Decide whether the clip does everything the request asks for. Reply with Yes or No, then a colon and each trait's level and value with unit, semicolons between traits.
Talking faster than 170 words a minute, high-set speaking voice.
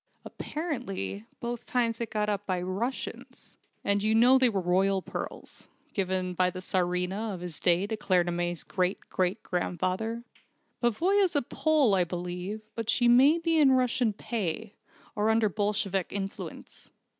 No: average, 155 wpm; high, 205 Hz